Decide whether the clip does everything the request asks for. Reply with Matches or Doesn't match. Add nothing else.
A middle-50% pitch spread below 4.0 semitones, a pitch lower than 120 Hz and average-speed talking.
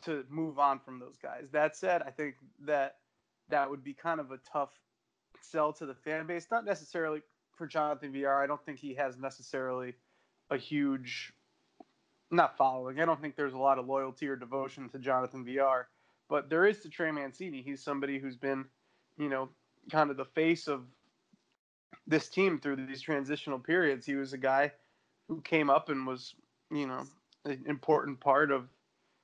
Doesn't match